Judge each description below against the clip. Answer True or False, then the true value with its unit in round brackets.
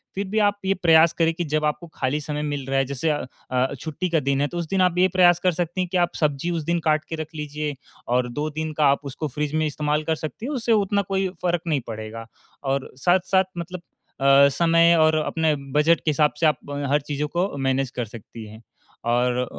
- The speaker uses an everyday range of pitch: True (3.8 semitones)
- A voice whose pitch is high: False (155 Hz)